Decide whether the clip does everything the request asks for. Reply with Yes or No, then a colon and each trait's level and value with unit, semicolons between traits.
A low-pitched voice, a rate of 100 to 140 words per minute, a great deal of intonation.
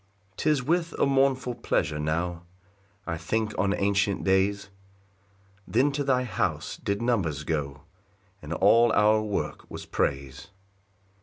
Yes: low, 100 Hz; slow, 135 wpm; wide, 7.0 semitones